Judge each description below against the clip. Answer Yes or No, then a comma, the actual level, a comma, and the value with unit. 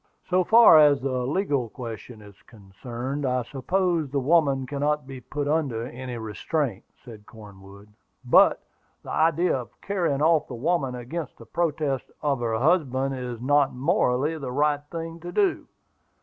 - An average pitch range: Yes, average, 4.2 semitones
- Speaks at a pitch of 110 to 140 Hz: Yes, low, 135 Hz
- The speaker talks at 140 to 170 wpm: Yes, average, 155 wpm